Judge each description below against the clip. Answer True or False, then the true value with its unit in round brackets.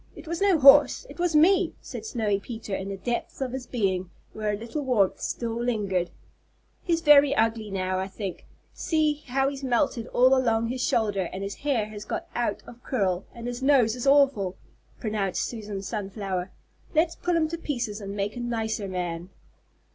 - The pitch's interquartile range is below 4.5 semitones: False (5.3 semitones)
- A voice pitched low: False (230 Hz)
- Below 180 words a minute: False (185 wpm)